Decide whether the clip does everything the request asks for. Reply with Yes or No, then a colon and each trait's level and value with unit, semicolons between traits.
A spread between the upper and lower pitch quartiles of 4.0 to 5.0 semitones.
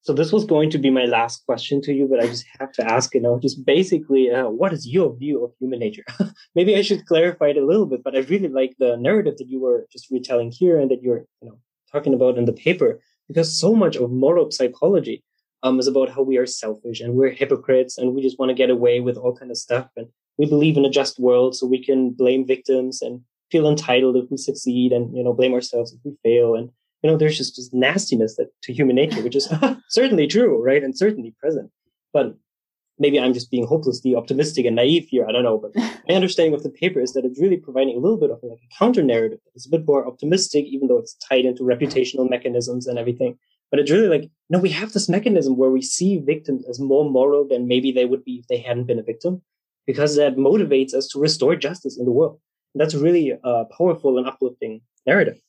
No: average, 3.6 semitones